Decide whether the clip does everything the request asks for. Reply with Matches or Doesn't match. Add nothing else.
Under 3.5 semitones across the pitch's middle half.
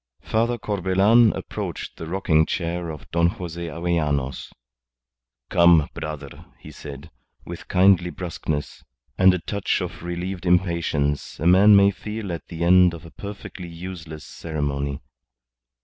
Matches